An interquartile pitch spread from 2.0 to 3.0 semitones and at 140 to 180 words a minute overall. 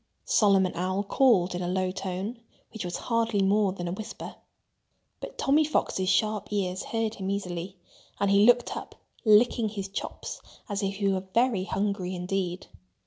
Yes: narrow, 2.5 semitones; average, 165 wpm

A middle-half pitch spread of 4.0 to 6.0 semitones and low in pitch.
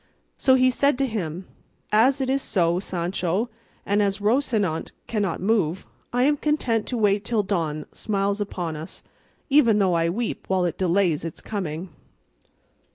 No: average, 5.1 semitones; high, 200 Hz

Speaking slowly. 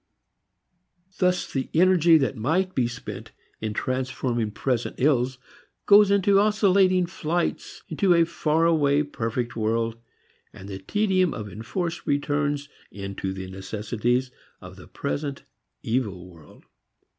Yes: slow, 120 wpm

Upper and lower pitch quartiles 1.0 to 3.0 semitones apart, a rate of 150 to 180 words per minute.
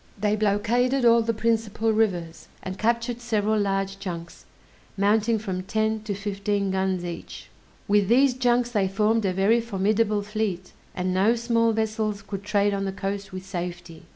Yes: narrow, 2.5 semitones; average, 160 wpm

